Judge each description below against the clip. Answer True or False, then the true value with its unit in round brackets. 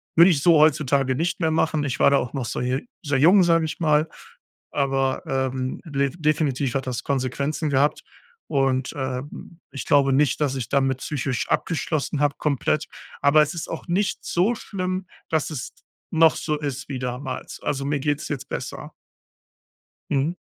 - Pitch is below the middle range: False (145 Hz)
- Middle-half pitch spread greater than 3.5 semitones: False (2.9 semitones)